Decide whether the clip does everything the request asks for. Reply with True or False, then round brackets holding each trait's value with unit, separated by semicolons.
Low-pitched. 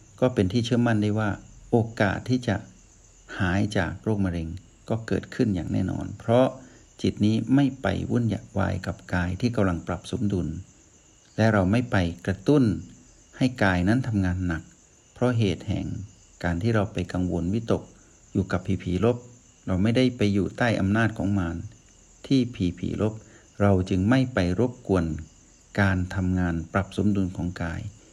True (100 Hz)